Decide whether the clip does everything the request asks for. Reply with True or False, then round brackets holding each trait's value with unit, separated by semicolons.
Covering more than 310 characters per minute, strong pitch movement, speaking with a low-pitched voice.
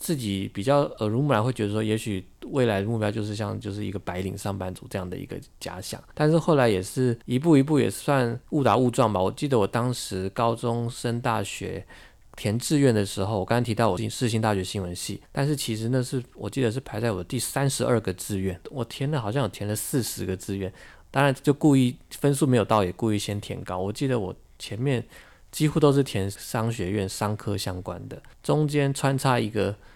False (320 characters per minute; 4.7 semitones; 115 Hz)